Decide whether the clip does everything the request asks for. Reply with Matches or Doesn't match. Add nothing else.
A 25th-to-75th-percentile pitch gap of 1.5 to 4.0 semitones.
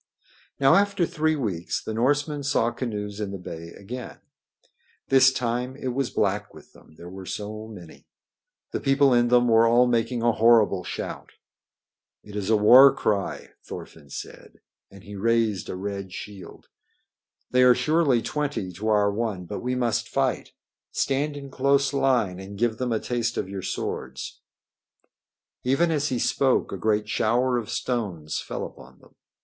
Doesn't match